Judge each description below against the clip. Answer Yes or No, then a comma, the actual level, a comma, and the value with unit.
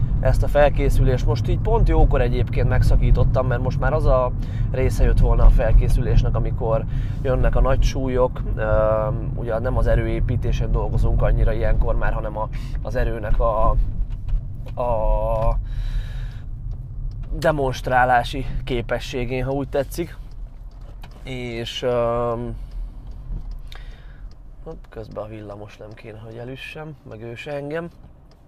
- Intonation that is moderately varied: No, narrow, 2.2 semitones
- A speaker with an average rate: Yes, average, 120 wpm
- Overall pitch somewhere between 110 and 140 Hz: Yes, low, 120 Hz